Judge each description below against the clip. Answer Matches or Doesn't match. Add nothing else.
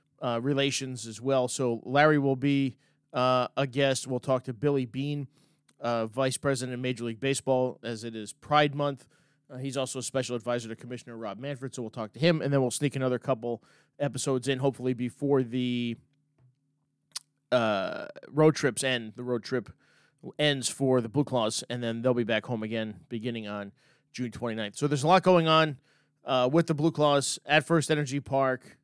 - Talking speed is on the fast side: Doesn't match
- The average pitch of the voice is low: Matches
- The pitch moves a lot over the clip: Doesn't match